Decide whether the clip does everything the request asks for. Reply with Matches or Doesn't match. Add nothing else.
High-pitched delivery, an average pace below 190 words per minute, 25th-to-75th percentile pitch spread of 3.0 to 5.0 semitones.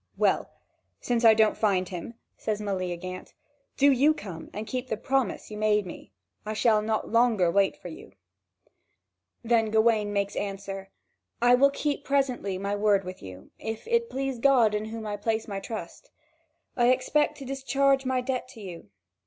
Matches